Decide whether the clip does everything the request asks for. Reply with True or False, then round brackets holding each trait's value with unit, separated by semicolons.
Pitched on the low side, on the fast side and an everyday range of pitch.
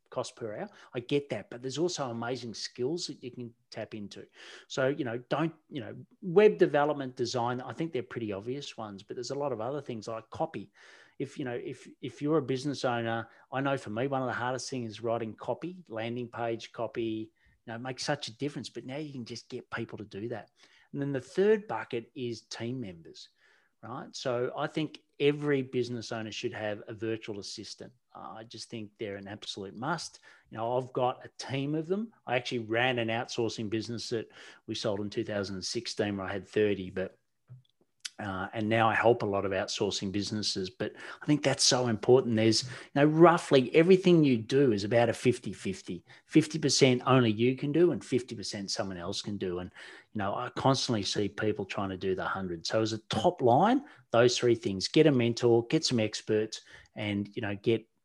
True (120 Hz; 210 wpm; 3.8 semitones)